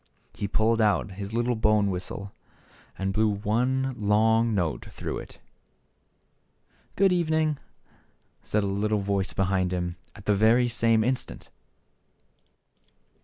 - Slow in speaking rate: Yes, slow, 125 wpm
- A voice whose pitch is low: Yes, low, 105 Hz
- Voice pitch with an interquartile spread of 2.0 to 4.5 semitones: Yes, average, 2.9 semitones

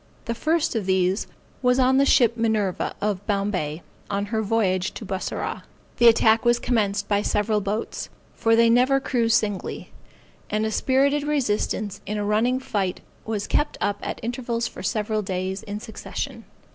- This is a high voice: Yes, high, 220 Hz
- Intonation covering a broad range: No, average, 2.8 semitones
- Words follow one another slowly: No, average, 165 wpm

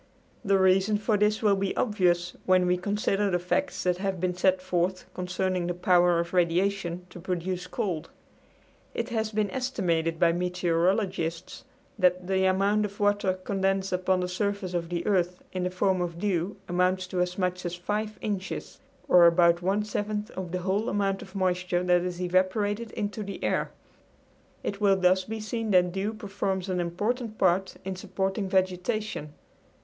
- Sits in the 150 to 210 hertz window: Yes, medium, 185 Hz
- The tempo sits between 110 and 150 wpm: No, average, 170 wpm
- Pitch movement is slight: Yes, narrow, 2.1 semitones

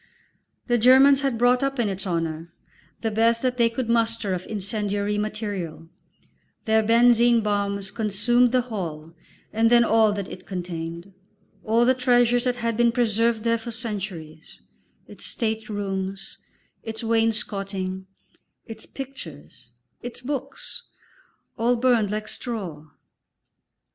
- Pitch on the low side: No, high, 220 Hz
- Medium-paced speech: No, slow, 130 wpm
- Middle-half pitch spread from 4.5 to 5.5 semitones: No, average, 3.4 semitones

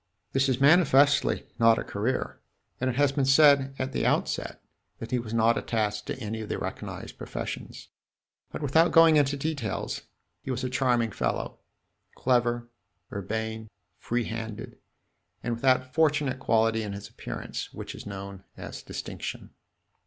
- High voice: No, low, 125 Hz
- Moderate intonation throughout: Yes, average, 3.5 semitones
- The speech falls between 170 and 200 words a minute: No, average, 155 wpm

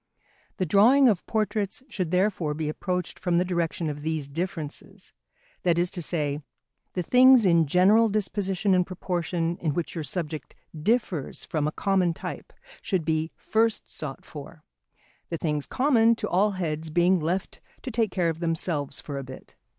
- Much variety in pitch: No, average, 4.0 semitones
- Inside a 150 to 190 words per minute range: Yes, average, 165 wpm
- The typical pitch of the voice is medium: Yes, medium, 175 Hz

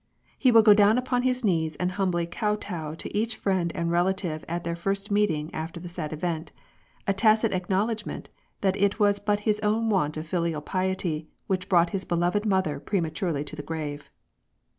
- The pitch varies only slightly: No, average, 3.8 semitones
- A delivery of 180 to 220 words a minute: Yes, average, 185 wpm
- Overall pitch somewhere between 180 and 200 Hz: Yes, medium, 185 Hz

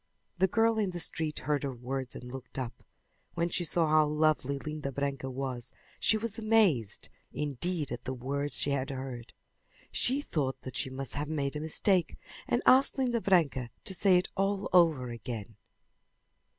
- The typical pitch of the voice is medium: Yes, medium, 150 Hz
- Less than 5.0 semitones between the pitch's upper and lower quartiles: No, wide, 5.5 semitones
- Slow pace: No, average, 175 wpm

